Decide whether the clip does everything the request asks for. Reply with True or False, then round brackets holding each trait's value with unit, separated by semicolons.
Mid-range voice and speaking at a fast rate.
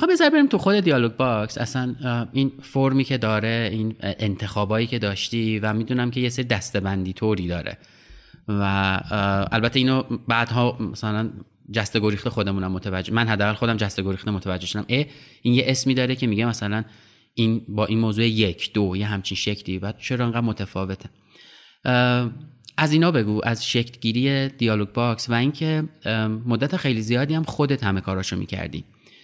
False (115 Hz; 160 wpm)